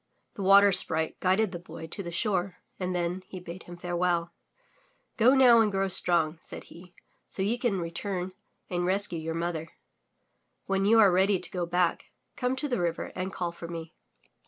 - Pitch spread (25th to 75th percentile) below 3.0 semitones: Yes, narrow, 2.5 semitones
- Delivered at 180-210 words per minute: Yes, average, 185 wpm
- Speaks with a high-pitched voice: No, medium, 180 Hz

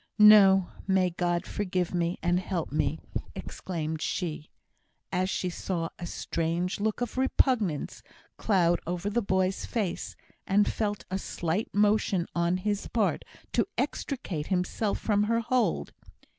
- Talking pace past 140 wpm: No, slow, 135 wpm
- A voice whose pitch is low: No, medium, 185 Hz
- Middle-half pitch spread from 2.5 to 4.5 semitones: Yes, average, 3.1 semitones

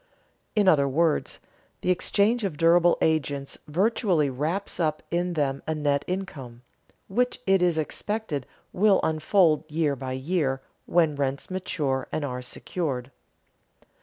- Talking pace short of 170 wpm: Yes, slow, 135 wpm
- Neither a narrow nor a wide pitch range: Yes, average, 4.6 semitones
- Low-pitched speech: No, medium, 160 Hz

